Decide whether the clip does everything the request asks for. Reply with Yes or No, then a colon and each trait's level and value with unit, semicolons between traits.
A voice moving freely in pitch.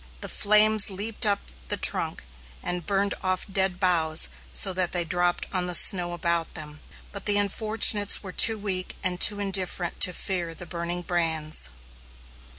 No: narrow, 2.6 semitones